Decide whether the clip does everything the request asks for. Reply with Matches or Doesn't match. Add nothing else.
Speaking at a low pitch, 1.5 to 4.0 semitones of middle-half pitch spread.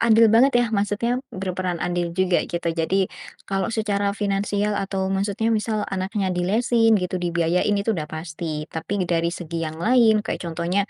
Doesn't match